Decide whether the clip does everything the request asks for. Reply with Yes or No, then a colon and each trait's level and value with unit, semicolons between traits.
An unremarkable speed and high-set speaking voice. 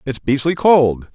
No: average, 160 wpm; low, 135 Hz